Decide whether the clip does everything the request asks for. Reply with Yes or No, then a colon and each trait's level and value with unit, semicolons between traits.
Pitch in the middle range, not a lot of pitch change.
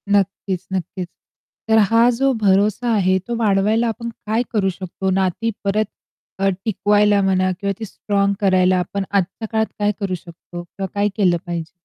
No: high, 200 Hz; narrow, 2.3 semitones